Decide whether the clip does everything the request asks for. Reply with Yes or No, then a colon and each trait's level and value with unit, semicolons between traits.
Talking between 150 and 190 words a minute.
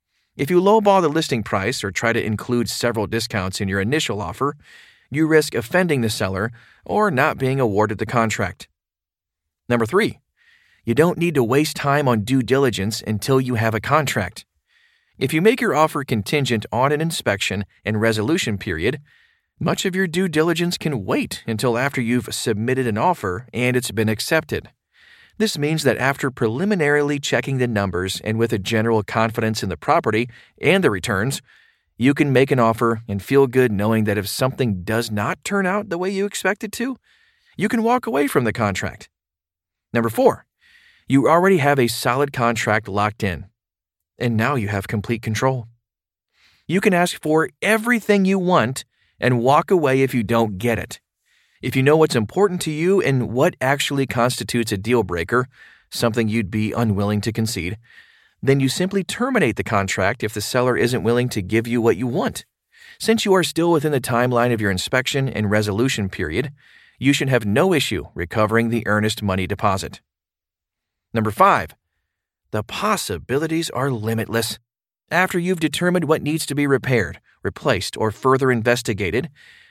Yes: average, 170 wpm